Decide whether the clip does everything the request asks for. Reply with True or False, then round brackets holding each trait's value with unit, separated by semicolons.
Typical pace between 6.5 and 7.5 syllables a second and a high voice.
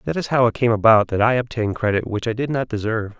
False (6.8 syllables/s; 115 Hz)